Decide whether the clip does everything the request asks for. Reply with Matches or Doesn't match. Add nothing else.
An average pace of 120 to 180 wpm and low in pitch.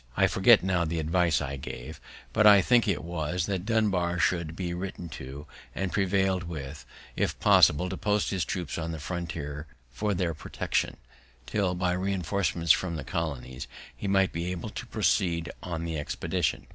Matches